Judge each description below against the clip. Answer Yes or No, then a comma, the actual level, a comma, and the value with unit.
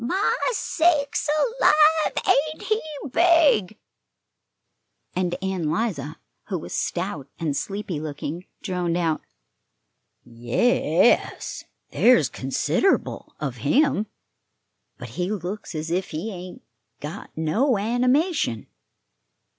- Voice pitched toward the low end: No, high, 190 Hz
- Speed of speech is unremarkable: No, slow, 100 wpm